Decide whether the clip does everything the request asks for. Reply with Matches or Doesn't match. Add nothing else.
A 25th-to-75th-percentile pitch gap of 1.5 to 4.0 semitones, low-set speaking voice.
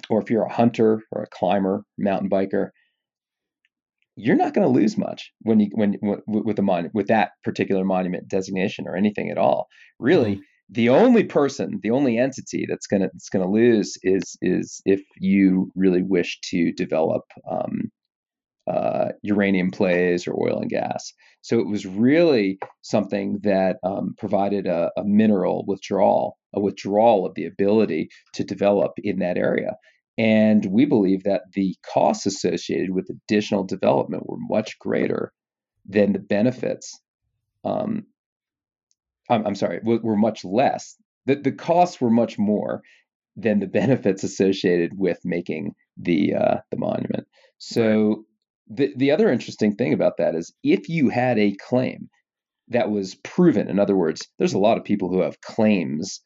Matches